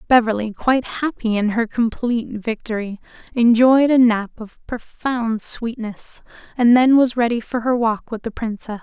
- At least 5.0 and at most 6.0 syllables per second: No, 4.6 syllables/s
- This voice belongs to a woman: Yes, female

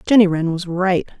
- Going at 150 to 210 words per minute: Yes, average, 200 wpm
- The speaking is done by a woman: Yes, female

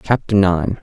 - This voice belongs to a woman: No, male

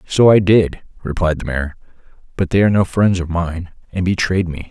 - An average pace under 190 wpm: No, fast, 205 wpm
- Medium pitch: No, very low, 90 Hz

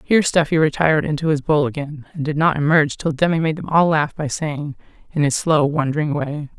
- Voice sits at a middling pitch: Yes, medium, 150 Hz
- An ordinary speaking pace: No, fast, 220 wpm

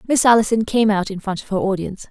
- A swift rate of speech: Yes, fast, 255 wpm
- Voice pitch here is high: Yes, high, 210 Hz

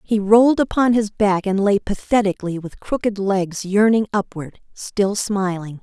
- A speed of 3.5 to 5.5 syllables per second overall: Yes, 4.5 syllables/s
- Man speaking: No, female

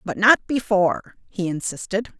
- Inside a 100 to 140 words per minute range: Yes, slow, 135 wpm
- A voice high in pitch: Yes, high, 200 Hz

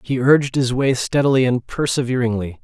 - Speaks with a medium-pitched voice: No, low, 130 Hz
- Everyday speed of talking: Yes, average, 160 wpm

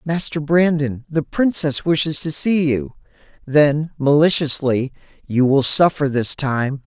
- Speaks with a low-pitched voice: No, medium, 145 Hz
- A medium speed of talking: No, slow, 130 wpm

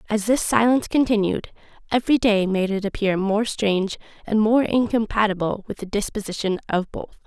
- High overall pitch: Yes, high, 210 Hz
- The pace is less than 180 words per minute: Yes, average, 155 wpm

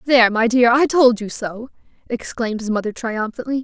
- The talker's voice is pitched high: Yes, high, 235 Hz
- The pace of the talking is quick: No, average, 180 wpm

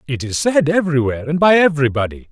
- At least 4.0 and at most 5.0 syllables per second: No, 7.0 syllables/s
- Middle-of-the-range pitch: Yes, medium, 150 Hz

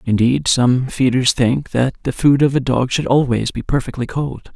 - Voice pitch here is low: Yes, low, 130 Hz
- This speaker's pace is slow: No, average, 200 wpm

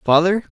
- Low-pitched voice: No, medium, 180 Hz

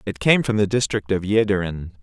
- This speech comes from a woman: No, male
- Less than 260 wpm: Yes, fast, 205 wpm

